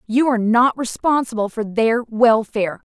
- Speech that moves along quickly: No, average, 145 wpm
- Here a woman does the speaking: Yes, female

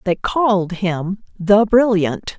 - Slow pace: Yes, slow, 125 wpm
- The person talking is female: Yes, female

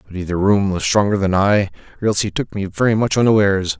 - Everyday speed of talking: No, fast, 235 wpm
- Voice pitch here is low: Yes, low, 100 Hz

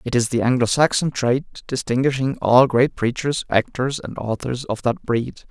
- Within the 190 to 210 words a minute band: No, average, 175 wpm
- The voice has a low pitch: Yes, low, 125 Hz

